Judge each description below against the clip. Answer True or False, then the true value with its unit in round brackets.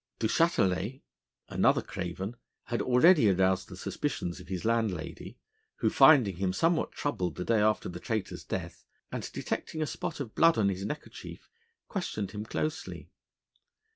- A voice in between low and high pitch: False (110 Hz)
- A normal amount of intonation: False (6.6 semitones)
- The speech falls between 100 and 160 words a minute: True (150 wpm)